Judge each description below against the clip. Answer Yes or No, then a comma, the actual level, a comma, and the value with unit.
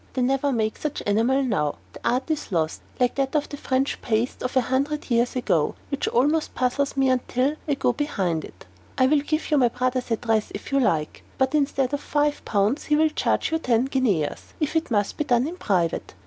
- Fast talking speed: Yes, fast, 220 wpm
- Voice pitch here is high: Yes, very high, 260 Hz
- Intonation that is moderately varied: Yes, average, 4.1 semitones